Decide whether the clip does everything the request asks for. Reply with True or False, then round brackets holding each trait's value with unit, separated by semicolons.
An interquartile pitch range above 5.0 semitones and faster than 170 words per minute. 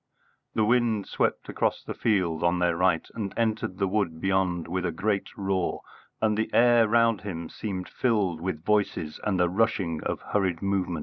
False (3.6 semitones; 180 wpm)